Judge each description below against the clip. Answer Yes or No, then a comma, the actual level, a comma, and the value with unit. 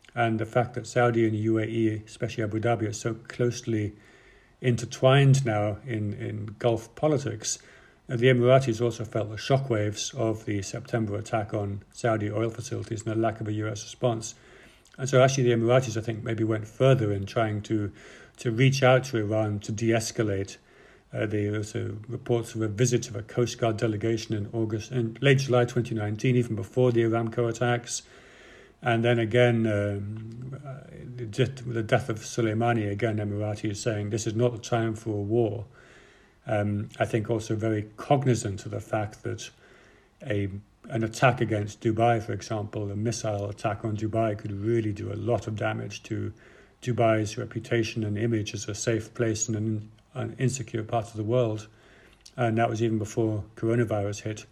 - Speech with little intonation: Yes, narrow, 1.9 semitones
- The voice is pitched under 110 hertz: No, low, 115 Hz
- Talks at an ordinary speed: Yes, average, 175 wpm